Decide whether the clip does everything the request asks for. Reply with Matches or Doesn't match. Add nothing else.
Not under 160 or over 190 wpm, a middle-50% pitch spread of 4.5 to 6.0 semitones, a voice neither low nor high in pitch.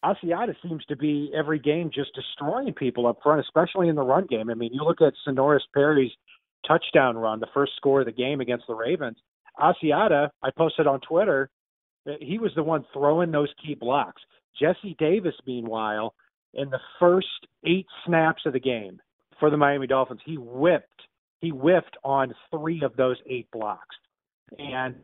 Doesn't match